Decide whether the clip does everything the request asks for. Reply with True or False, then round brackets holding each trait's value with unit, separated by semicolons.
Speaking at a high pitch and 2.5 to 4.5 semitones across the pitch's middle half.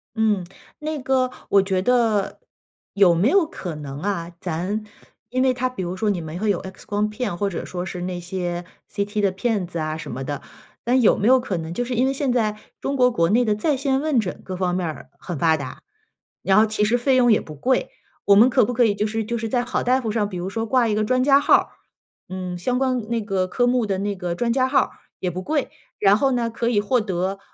False (210 Hz; 5.2 semitones)